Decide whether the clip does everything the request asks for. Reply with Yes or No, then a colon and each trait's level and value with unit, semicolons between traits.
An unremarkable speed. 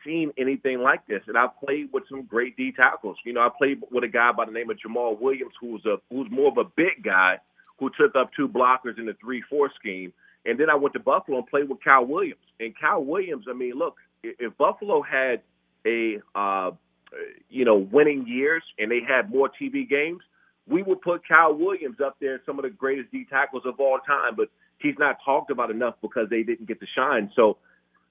No: fast, 220 wpm